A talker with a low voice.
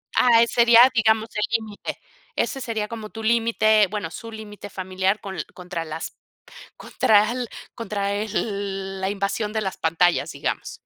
No: high, 210 Hz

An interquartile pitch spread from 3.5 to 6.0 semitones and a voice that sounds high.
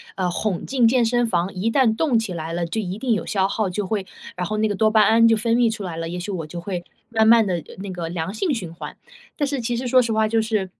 Yes: average, 4.2 semitones; high, 215 Hz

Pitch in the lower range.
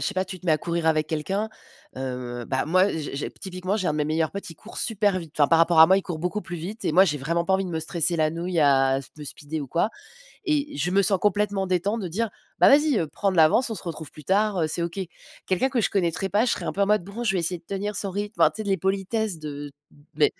No: medium, 180 Hz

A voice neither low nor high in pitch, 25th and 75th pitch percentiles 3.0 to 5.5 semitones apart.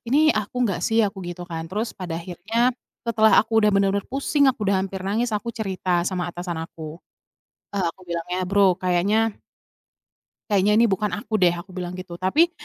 No: high, 195 Hz; average, 3.6 semitones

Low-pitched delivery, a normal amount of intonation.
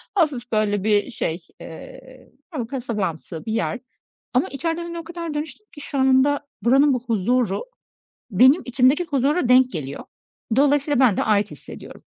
No: very high, 260 Hz; average, 5.0 semitones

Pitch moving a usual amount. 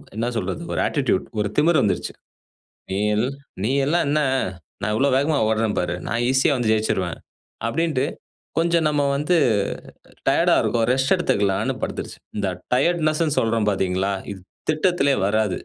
No: wide, 6.5 semitones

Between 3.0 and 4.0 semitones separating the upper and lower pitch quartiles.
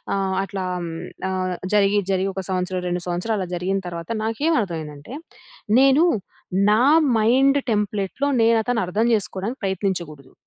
Yes: average, 3.7 semitones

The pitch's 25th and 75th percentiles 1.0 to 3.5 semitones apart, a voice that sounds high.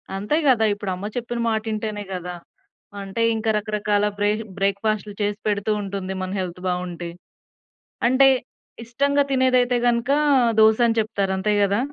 Yes: average, 3.1 semitones; high, 210 Hz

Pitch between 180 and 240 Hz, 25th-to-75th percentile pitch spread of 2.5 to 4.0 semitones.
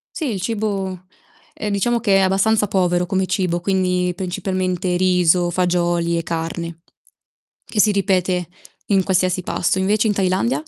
No: medium, 185 Hz; narrow, 1.8 semitones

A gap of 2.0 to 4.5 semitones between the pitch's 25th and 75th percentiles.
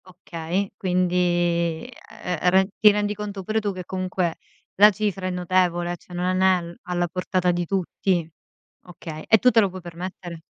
No: narrow, 1.6 semitones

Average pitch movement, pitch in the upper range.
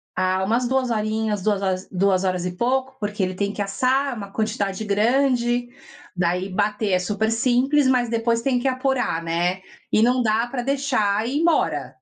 Yes: average, 4.5 semitones; high, 220 Hz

